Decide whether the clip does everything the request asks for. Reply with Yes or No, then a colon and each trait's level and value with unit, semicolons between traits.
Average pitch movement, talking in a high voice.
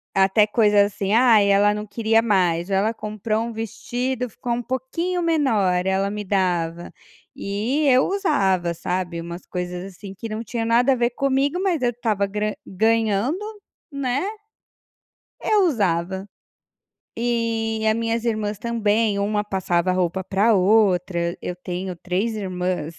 Yes: average, 3.8 semitones; high, 210 Hz